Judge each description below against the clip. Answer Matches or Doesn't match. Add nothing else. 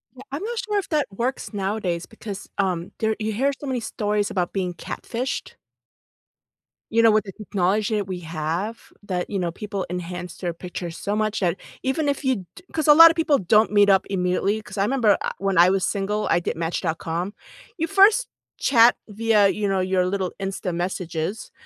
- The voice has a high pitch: Matches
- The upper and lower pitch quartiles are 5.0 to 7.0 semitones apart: Doesn't match